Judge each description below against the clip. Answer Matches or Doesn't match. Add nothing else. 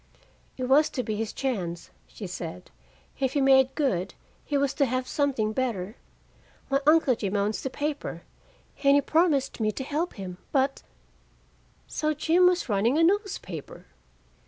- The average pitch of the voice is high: Matches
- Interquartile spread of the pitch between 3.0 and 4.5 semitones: Doesn't match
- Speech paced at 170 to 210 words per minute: Doesn't match